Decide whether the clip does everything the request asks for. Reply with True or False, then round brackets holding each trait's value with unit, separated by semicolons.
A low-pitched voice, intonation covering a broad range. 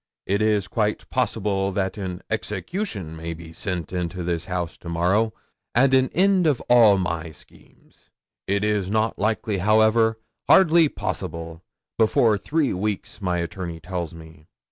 False (100 Hz; 4.3 semitones)